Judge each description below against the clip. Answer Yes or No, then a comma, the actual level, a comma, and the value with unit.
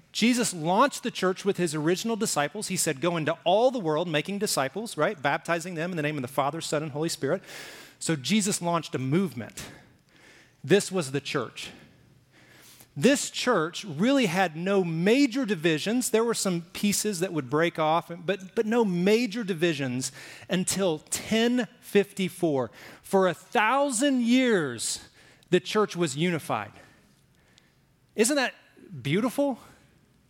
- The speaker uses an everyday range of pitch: No, wide, 5.7 semitones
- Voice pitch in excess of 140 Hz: Yes, medium, 185 Hz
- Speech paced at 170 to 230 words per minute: No, average, 145 wpm